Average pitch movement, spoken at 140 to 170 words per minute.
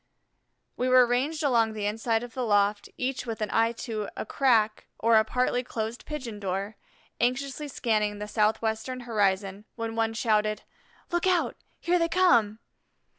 Yes: average, 3.0 semitones; average, 160 wpm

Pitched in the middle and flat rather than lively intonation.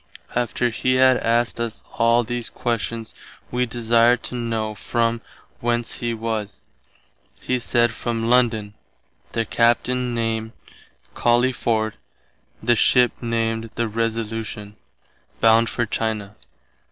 No: low, 115 Hz; narrow, 1.1 semitones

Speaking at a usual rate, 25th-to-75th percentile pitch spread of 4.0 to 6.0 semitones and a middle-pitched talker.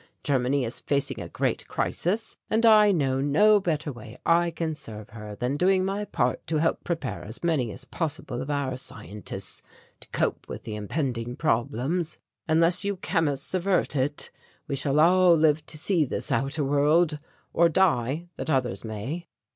Yes: average, 170 wpm; average, 4.9 semitones; medium, 150 Hz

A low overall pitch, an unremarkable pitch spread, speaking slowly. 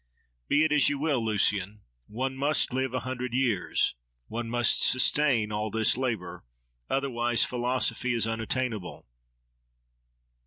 Yes: low, 120 Hz; average, 3.0 semitones; slow, 125 wpm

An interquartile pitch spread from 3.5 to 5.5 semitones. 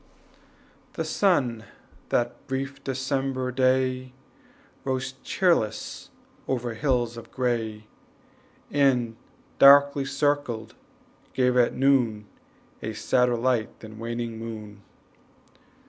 No: average, 2.8 semitones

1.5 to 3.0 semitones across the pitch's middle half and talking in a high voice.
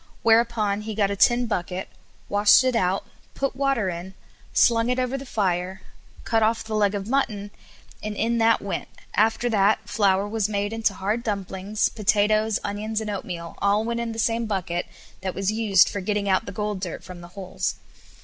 Yes: narrow, 2.6 semitones; high, 210 Hz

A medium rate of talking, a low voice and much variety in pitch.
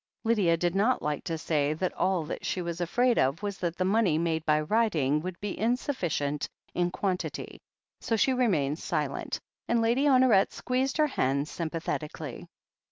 No: average, 170 wpm; medium, 180 Hz; wide, 6.6 semitones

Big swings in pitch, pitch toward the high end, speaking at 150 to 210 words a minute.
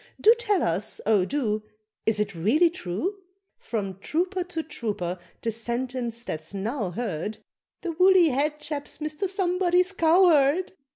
No: wide, 8.8 semitones; very high, 280 Hz; slow, 135 wpm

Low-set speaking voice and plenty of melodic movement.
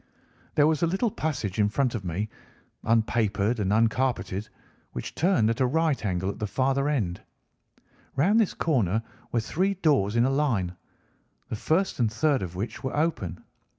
Yes: low, 120 Hz; wide, 6.5 semitones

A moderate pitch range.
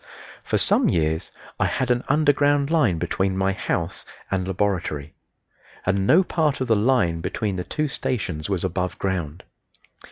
No: wide, 6.6 semitones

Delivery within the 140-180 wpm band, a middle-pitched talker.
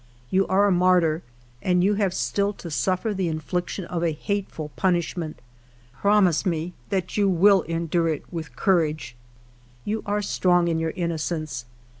Yes: average, 160 wpm; medium, 175 Hz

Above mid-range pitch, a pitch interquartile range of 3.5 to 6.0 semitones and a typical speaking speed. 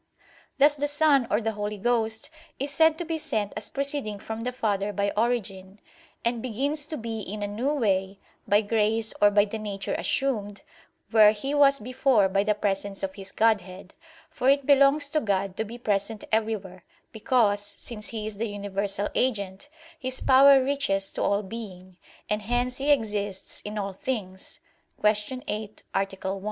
Yes: high, 215 Hz; average, 4.1 semitones; average, 175 wpm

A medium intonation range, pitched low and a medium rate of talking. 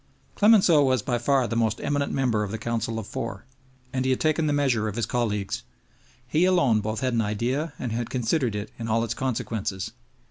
No: average, 3.8 semitones; low, 120 Hz; fast, 210 wpm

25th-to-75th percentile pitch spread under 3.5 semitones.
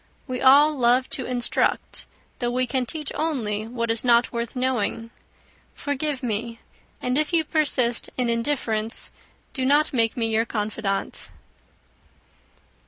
Yes: average, 2.9 semitones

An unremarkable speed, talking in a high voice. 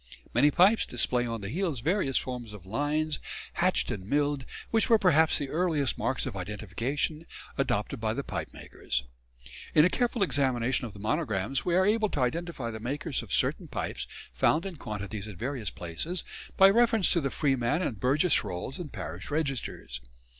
No: average, 175 wpm; medium, 140 Hz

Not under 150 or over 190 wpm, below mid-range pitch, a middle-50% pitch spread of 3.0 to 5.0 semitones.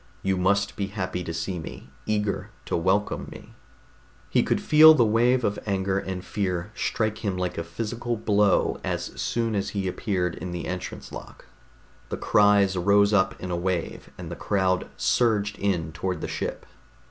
No: average, 175 wpm; low, 100 Hz; narrow, 2.4 semitones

